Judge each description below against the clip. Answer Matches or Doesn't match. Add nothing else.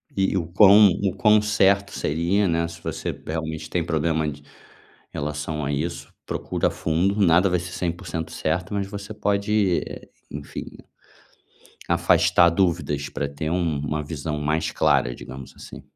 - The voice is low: Matches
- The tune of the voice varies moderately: Matches